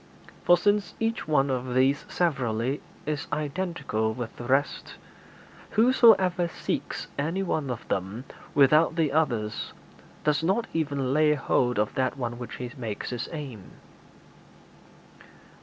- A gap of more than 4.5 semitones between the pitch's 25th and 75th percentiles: Yes, average, 5.0 semitones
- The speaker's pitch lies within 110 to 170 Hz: Yes, medium, 140 Hz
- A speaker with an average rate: No, slow, 130 wpm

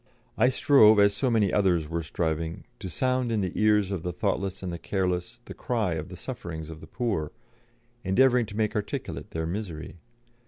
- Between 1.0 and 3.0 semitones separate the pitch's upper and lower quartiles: No, average, 4.6 semitones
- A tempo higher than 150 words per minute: Yes, average, 190 wpm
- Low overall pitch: Yes, very low, 95 Hz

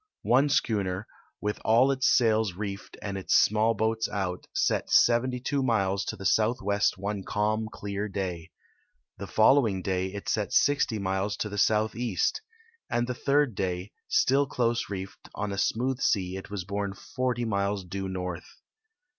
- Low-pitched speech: Yes, low, 105 Hz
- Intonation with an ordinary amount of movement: Yes, average, 3.4 semitones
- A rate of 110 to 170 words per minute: Yes, average, 155 wpm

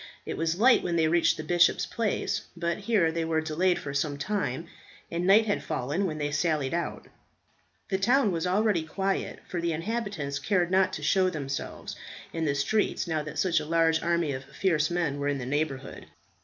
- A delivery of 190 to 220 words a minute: Yes, average, 195 wpm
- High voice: No, medium, 165 Hz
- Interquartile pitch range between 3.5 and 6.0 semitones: Yes, average, 4.0 semitones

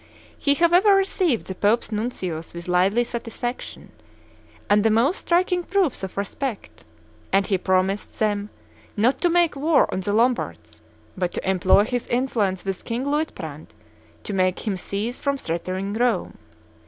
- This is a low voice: No, high, 220 Hz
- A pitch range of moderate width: No, wide, 6.3 semitones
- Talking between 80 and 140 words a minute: No, average, 150 wpm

